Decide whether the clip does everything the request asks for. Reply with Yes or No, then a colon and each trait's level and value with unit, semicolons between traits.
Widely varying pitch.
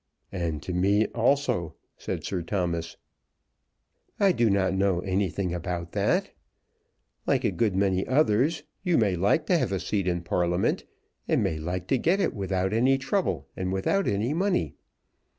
Yes: wide, 5.7 semitones